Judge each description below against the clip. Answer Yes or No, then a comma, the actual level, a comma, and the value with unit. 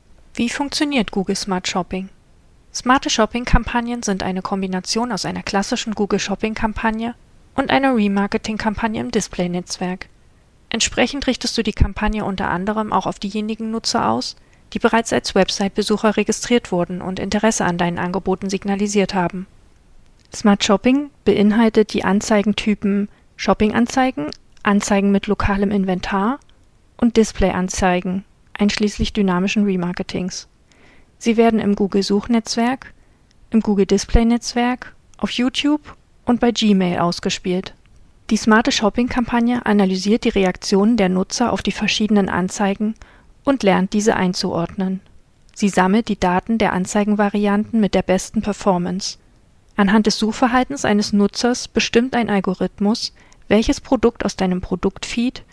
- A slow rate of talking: Yes, slow, 120 wpm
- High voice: Yes, high, 210 Hz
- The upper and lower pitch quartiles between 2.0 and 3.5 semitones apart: Yes, average, 3.0 semitones